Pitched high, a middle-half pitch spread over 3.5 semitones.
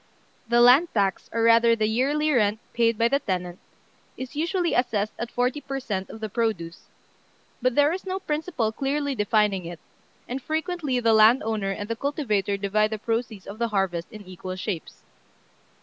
Yes: high, 230 Hz; average, 4.7 semitones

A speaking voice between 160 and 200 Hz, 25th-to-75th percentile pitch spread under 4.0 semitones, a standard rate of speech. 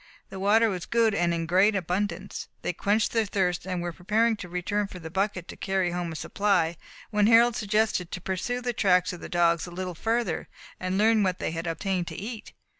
No: high, 190 Hz; average, 3.2 semitones; fast, 215 wpm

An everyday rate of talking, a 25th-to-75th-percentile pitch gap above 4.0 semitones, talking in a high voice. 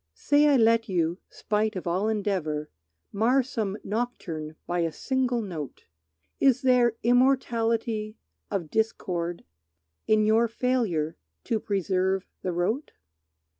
No: slow, 120 wpm; average, 5.0 semitones; high, 215 Hz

